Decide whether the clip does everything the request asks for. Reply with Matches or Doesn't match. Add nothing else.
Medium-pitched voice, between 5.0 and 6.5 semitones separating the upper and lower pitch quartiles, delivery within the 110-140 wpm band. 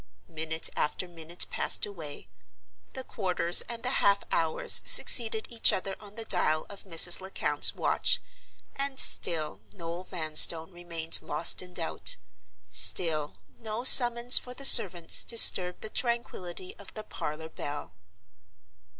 Matches